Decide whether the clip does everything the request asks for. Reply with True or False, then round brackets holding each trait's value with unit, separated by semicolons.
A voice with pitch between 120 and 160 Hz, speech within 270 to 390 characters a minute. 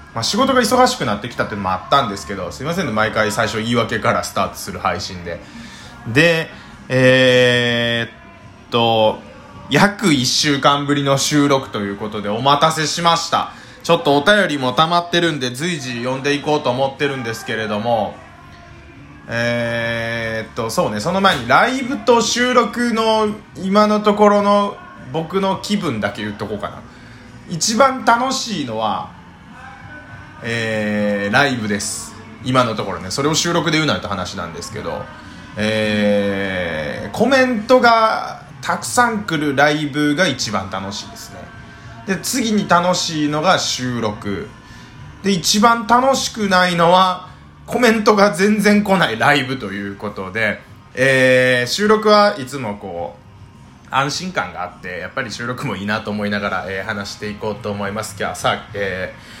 True (135 Hz; 305 characters per minute)